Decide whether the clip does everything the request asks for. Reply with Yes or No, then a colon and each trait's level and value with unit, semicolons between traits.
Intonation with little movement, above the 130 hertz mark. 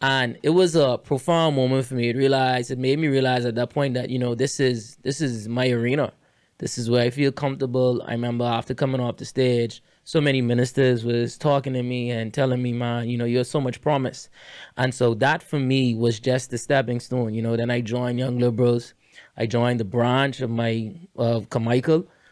No: narrow, 2.0 semitones; low, 125 Hz